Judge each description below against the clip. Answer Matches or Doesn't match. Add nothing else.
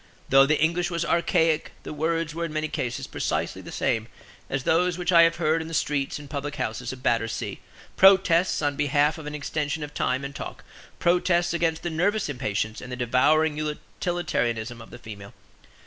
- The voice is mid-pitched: Matches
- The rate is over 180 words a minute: Matches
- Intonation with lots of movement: Doesn't match